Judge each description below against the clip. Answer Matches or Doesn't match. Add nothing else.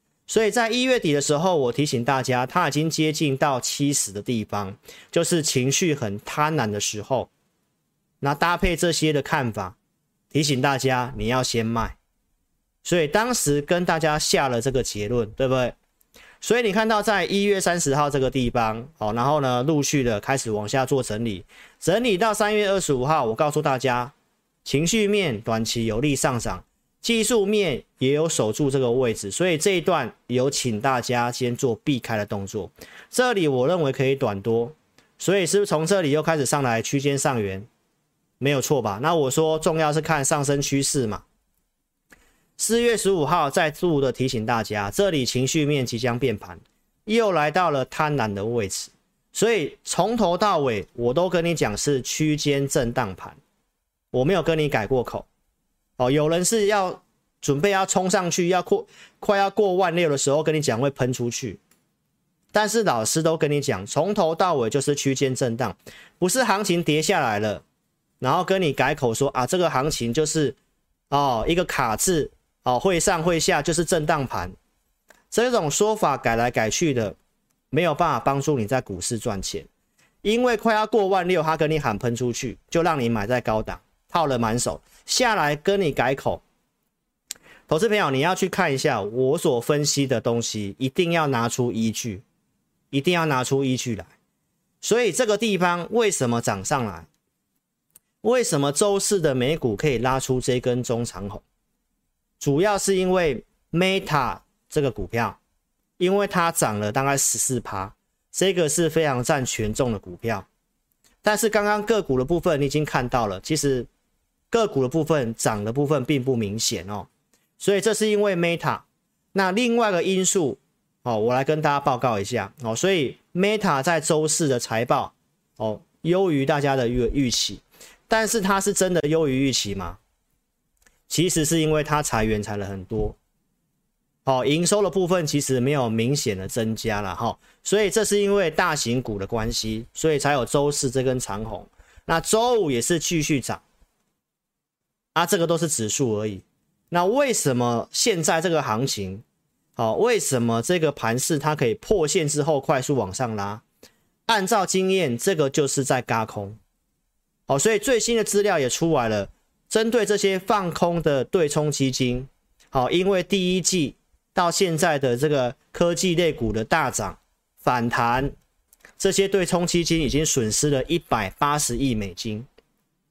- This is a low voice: Doesn't match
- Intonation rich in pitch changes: Matches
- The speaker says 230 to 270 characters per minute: Matches